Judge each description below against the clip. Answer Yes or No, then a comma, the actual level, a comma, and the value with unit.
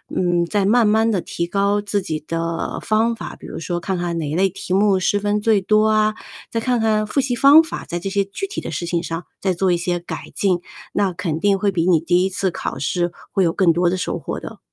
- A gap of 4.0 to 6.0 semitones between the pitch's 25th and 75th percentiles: No, average, 3.4 semitones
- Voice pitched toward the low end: No, high, 190 Hz